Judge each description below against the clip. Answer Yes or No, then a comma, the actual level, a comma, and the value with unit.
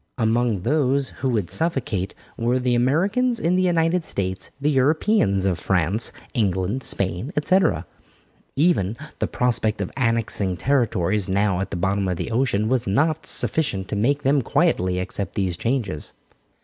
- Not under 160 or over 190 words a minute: No, average, 150 wpm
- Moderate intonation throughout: No, wide, 6.6 semitones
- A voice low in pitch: Yes, low, 115 Hz